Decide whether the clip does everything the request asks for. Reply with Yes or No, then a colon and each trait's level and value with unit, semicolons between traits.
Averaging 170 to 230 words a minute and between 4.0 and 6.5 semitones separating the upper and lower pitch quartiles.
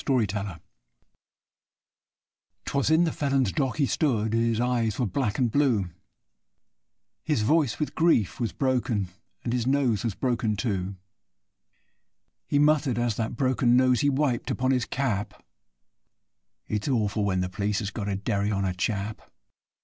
No: average, 160 wpm; average, 4.4 semitones